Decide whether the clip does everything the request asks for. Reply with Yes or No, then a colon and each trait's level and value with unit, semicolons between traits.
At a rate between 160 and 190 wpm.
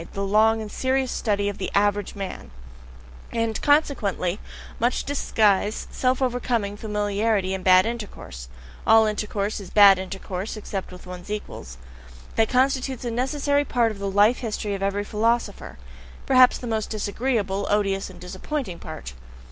No: average, 150 wpm